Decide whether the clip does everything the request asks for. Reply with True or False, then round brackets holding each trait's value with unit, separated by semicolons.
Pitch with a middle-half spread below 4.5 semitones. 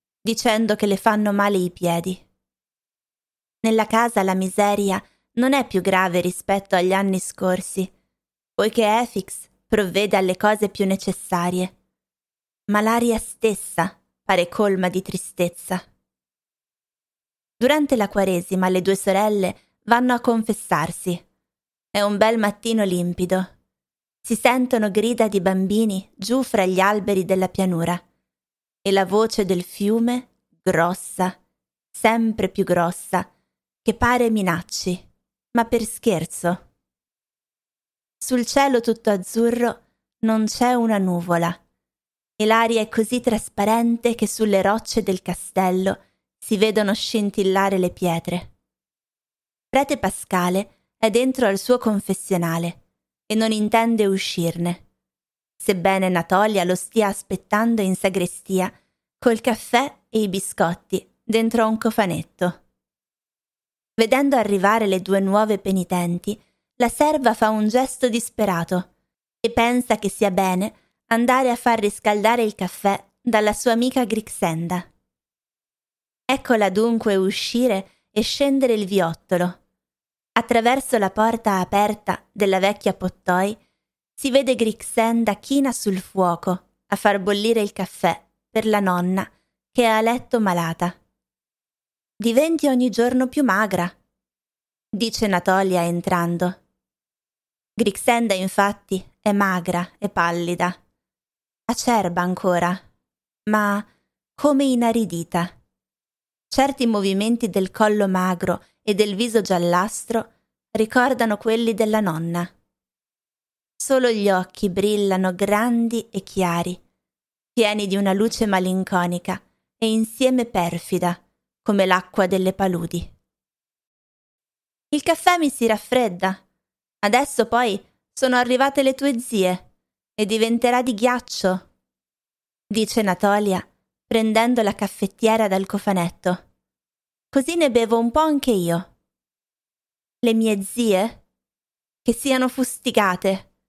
True (3.6 semitones)